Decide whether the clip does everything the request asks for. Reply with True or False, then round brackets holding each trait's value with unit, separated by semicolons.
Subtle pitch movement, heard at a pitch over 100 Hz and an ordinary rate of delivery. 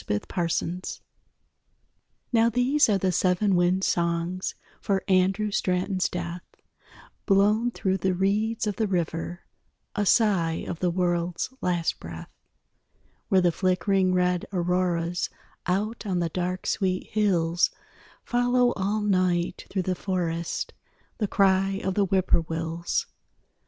False (2.3 semitones; 185 Hz; 130 wpm)